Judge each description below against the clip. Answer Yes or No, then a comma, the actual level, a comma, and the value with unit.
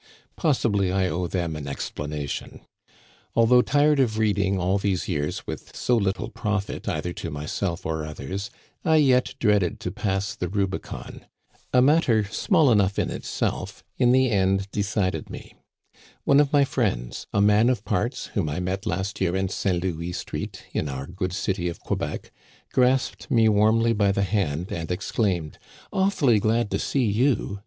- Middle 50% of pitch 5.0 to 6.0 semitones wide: No, average, 4.5 semitones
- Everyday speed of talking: Yes, average, 165 wpm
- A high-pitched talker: No, low, 100 Hz